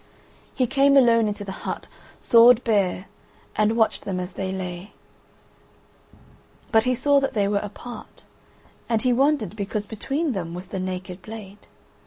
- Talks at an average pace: Yes, average, 155 wpm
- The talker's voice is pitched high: Yes, high, 215 Hz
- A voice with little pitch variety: No, average, 4.3 semitones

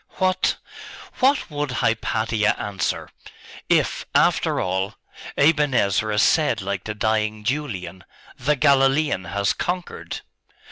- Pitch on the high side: No, low, 110 Hz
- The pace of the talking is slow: Yes, slow, 105 wpm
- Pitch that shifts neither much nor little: No, wide, 6.5 semitones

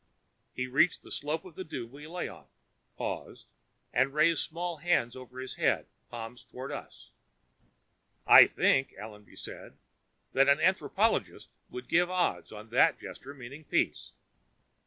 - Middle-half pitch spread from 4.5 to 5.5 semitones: Yes, average, 5.0 semitones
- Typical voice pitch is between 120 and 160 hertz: Yes, medium, 140 Hz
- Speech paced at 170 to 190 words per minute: No, average, 145 wpm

